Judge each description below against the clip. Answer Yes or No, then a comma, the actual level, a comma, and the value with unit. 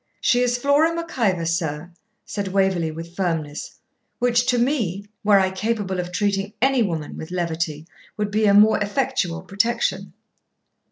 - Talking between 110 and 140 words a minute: No, average, 155 wpm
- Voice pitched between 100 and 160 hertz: No, high, 200 Hz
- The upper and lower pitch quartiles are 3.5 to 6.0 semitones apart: Yes, wide, 5.5 semitones